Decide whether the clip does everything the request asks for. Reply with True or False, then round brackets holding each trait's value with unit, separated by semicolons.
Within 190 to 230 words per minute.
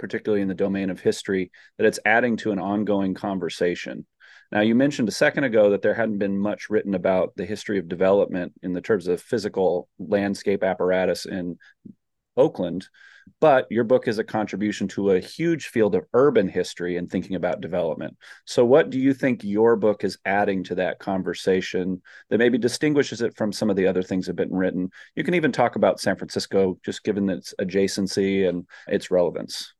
True (195 wpm)